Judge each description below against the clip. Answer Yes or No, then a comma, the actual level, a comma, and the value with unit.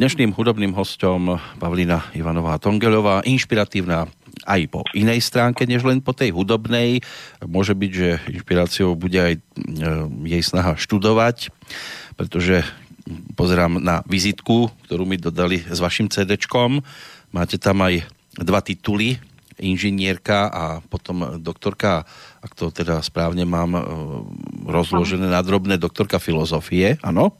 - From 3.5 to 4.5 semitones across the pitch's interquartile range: Yes, average, 3.8 semitones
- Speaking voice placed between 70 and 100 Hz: Yes, very low, 95 Hz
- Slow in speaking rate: No, average, 120 wpm